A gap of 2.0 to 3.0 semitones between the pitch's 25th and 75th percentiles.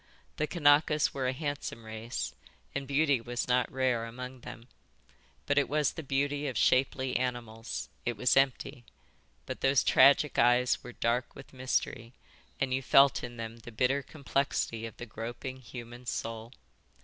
Yes: narrow, 2.6 semitones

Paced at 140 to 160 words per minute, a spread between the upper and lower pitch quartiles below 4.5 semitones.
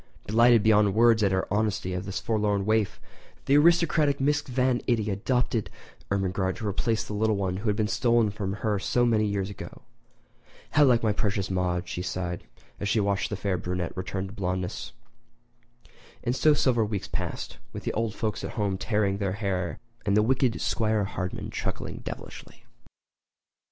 No: average, 175 wpm; average, 3.0 semitones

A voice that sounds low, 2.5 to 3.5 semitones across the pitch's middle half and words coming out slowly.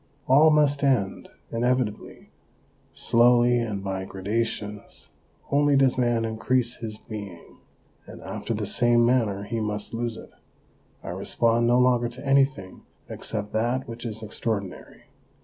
Yes: low, 115 Hz; average, 2.9 semitones; slow, 130 wpm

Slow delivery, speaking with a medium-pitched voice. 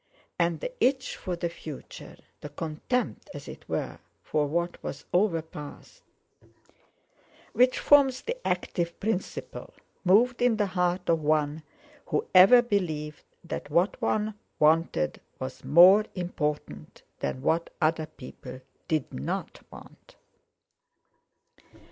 Yes: slow, 120 wpm; medium, 170 Hz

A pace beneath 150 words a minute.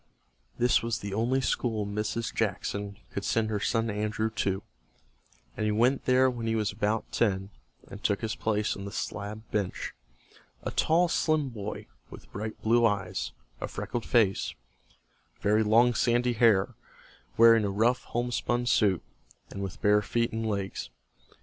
No: average, 155 wpm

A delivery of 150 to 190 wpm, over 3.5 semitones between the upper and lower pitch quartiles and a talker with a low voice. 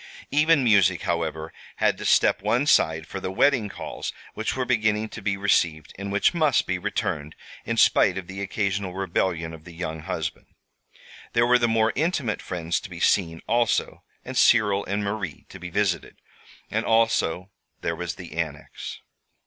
Yes: average, 175 wpm; average, 4.9 semitones; low, 100 Hz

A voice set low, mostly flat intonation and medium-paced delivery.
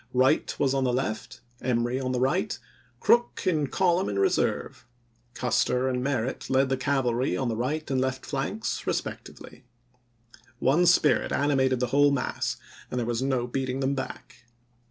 Yes: low, 130 Hz; narrow, 1.8 semitones; average, 165 wpm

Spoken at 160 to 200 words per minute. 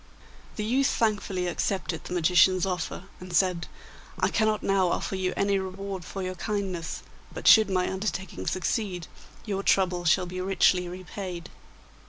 No: average, 150 wpm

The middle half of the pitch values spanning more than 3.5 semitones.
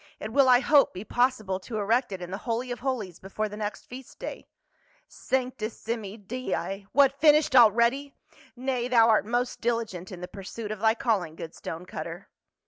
Yes: average, 4.3 semitones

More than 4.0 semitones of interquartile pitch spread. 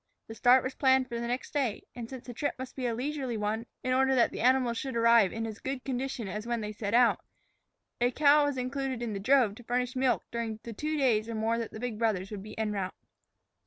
No: average, 2.8 semitones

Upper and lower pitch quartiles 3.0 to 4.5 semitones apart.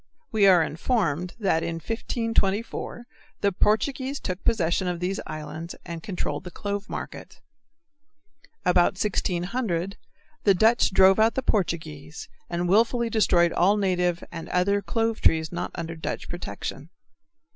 Yes: average, 4.0 semitones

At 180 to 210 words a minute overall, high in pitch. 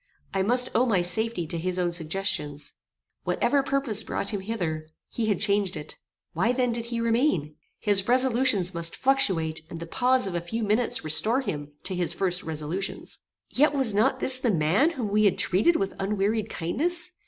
Yes: average, 185 wpm; high, 205 Hz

